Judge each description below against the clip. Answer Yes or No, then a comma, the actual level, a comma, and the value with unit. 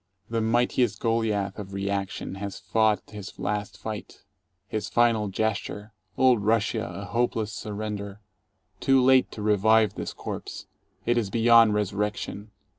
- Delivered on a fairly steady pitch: Yes, narrow, 2.0 semitones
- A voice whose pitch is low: Yes, low, 105 Hz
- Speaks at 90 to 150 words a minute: Yes, slow, 135 wpm